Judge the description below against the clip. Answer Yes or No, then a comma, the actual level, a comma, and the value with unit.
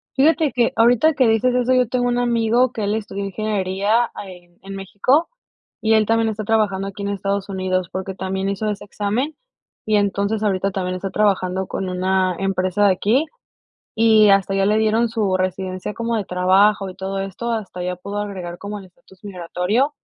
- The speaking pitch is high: Yes, high, 200 Hz